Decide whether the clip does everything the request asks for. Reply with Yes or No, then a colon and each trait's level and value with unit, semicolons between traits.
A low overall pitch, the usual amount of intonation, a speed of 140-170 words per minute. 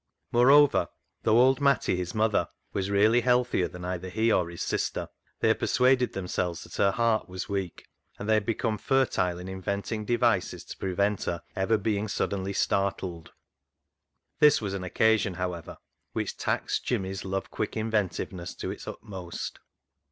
Yes: low, 100 Hz; average, 3.5 semitones; average, 160 wpm